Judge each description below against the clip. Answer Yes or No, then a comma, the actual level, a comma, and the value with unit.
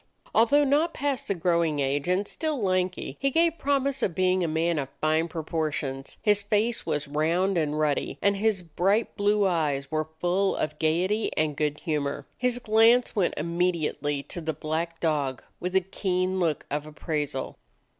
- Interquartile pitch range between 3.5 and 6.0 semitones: Yes, average, 5.0 semitones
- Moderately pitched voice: Yes, medium, 175 Hz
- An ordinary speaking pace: Yes, average, 170 wpm